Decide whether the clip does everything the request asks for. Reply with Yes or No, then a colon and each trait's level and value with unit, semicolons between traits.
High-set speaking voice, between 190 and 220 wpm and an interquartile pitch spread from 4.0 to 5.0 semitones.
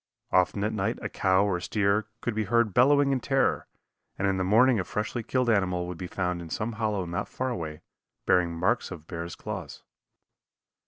No: low, 100 Hz; average, 195 wpm; average, 4.6 semitones